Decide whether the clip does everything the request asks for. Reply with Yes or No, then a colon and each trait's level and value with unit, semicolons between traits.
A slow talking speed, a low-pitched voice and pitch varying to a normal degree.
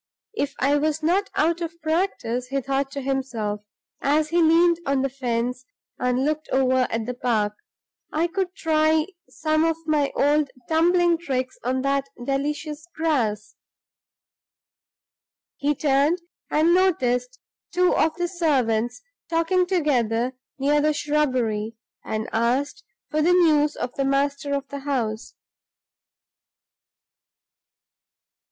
No: slow, 120 wpm; very high, 285 Hz; average, 4.0 semitones